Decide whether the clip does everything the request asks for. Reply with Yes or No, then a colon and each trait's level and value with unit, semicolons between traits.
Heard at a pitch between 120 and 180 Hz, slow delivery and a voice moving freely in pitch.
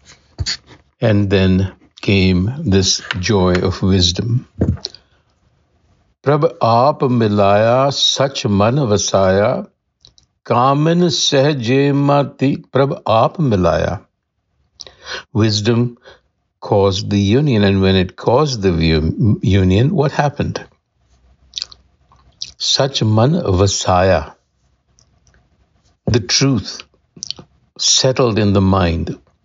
No: low, 100 Hz; slow, 75 wpm; wide, 6.0 semitones